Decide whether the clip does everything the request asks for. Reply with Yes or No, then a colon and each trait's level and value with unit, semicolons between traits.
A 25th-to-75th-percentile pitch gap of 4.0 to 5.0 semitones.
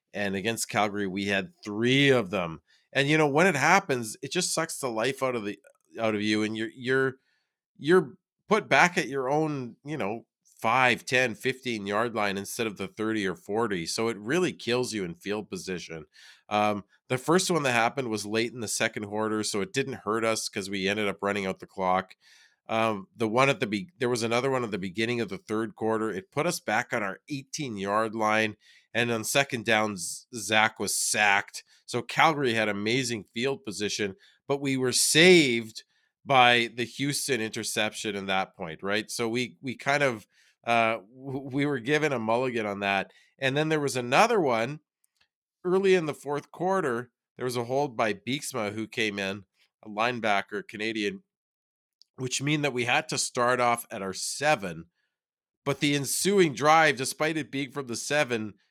Yes: average, 4.5 semitones